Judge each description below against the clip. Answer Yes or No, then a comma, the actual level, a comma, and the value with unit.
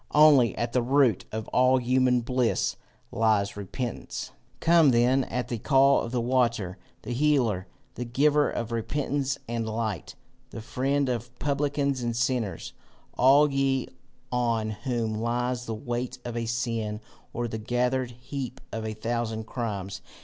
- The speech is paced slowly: No, average, 150 wpm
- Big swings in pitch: No, narrow, 2.6 semitones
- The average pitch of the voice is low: Yes, low, 120 Hz